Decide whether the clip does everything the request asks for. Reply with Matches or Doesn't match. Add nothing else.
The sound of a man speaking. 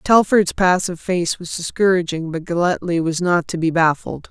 Doesn't match